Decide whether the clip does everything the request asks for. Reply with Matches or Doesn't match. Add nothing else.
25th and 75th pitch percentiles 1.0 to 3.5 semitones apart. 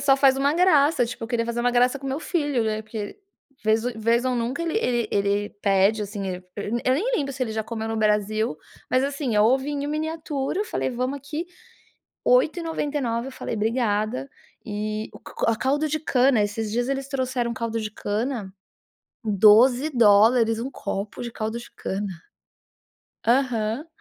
Doesn't match